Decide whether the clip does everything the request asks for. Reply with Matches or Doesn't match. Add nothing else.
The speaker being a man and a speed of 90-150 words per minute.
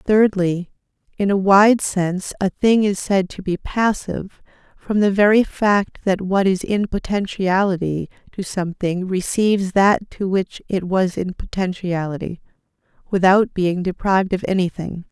Doesn't match